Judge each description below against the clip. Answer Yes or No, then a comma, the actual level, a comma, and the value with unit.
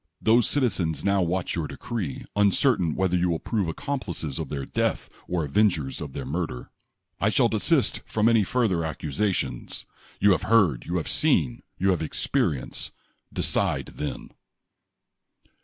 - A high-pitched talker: No, very low, 90 Hz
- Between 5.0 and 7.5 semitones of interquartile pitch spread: Yes, wide, 5.6 semitones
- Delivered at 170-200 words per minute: No, average, 145 wpm